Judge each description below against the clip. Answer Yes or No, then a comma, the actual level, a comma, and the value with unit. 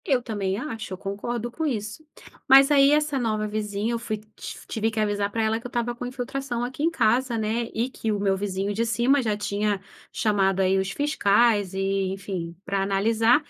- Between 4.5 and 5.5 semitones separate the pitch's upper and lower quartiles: No, average, 3.3 semitones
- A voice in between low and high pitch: No, high, 220 Hz